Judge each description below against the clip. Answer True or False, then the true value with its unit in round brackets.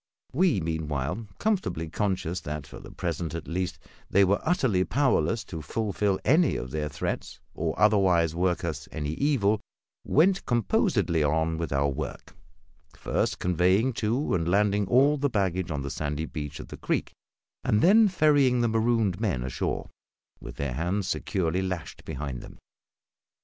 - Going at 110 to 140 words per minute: False (155 wpm)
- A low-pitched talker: True (95 Hz)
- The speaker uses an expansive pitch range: True (6.1 semitones)